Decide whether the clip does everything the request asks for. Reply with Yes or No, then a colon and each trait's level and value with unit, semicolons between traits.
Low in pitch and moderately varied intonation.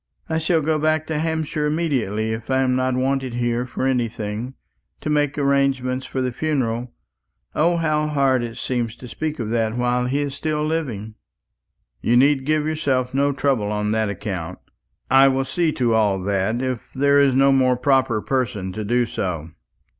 Yes: low, 130 Hz; average, 3.9 semitones